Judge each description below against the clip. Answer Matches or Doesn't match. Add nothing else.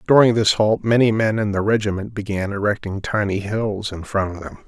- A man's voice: Matches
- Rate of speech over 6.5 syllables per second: Doesn't match